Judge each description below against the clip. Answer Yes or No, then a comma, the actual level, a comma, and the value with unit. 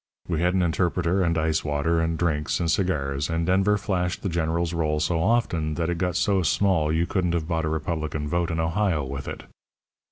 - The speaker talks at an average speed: No, fast, 210 wpm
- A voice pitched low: Yes, very low, 85 Hz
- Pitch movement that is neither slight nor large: No, narrow, 2.3 semitones